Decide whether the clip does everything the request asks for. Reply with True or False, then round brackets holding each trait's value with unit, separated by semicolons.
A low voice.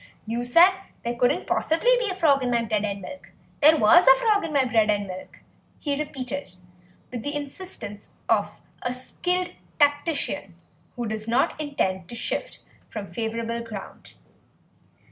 False (245 Hz)